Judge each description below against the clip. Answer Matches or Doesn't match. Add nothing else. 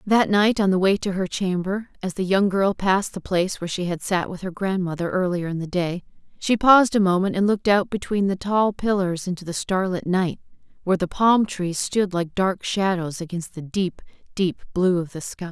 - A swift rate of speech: Matches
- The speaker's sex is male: Doesn't match